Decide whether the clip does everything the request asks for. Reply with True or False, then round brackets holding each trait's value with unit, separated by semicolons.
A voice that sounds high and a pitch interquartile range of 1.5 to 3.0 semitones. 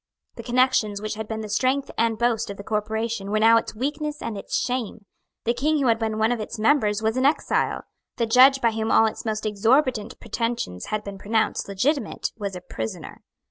True (225 Hz; 2.6 semitones)